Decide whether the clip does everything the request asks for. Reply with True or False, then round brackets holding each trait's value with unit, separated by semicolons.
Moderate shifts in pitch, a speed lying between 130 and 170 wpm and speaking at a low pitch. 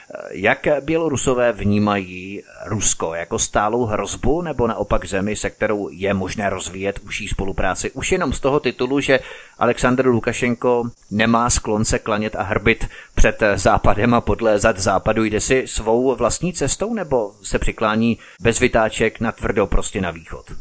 True (3.3 semitones; 150 wpm; 110 Hz)